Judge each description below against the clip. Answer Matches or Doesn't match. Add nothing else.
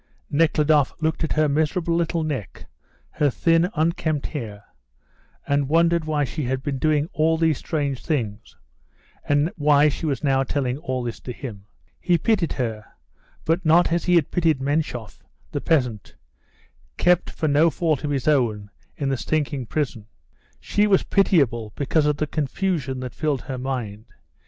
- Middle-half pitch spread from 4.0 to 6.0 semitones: Doesn't match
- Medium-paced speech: Matches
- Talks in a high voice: Doesn't match